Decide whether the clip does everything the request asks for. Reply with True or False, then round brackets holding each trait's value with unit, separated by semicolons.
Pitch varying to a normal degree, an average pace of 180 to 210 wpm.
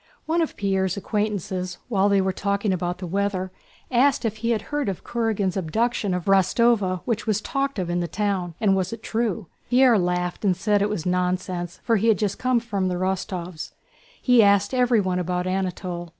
True (3.5 semitones; 195 wpm)